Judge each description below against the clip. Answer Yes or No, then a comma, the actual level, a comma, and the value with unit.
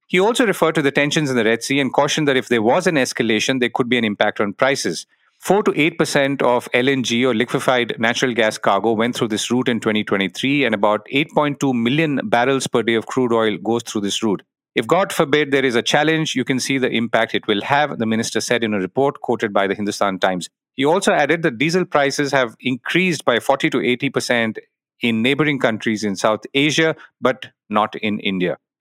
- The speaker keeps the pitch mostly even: No, average, 4.0 semitones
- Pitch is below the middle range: Yes, low, 125 Hz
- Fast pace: Yes, fast, 220 wpm